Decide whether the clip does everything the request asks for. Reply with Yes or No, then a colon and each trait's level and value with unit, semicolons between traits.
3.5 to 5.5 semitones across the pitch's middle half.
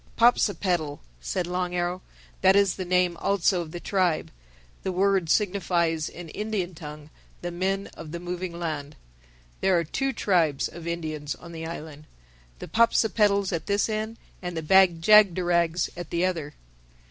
No: average, 2.7 semitones